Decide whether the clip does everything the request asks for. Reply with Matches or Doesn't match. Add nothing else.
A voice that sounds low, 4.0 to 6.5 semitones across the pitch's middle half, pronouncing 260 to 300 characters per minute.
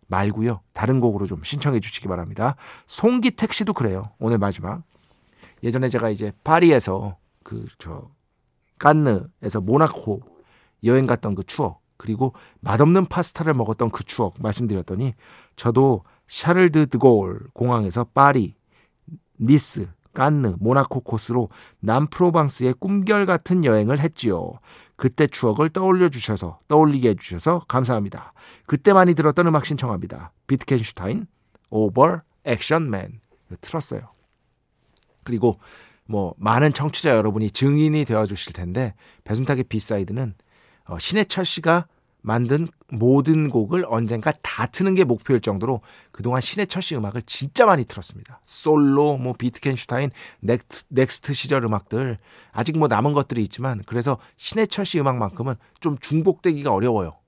Doesn't match